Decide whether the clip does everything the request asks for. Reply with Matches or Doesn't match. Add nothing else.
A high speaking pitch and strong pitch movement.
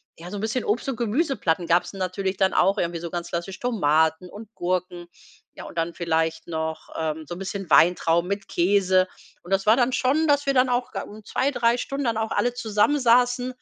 Matches